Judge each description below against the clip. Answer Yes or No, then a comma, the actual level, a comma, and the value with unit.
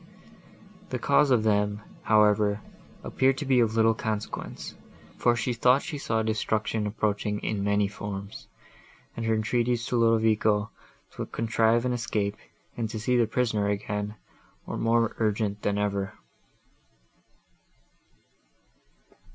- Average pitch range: No, narrow, 2.1 semitones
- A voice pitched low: Yes, low, 110 Hz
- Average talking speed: No, slow, 125 wpm